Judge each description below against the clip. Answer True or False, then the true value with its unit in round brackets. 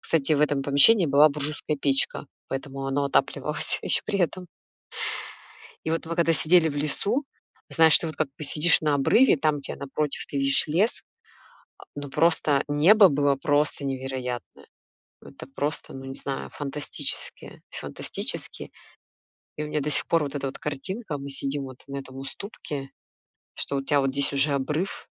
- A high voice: False (145 Hz)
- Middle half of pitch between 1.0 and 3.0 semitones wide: True (2.4 semitones)